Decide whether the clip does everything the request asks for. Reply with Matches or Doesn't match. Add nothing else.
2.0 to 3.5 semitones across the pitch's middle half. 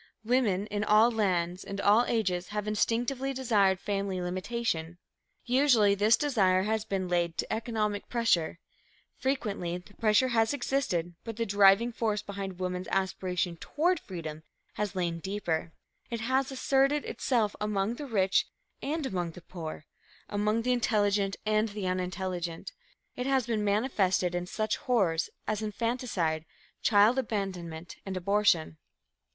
Doesn't match